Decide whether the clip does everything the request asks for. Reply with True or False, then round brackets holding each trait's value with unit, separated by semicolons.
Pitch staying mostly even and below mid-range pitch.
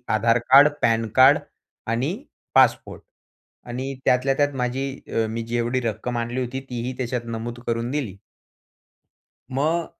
True (2.3 semitones; 120 Hz)